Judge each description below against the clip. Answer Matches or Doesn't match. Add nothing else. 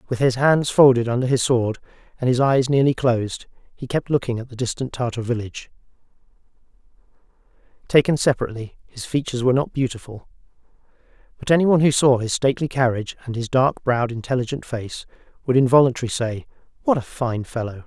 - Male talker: Matches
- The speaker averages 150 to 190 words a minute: Matches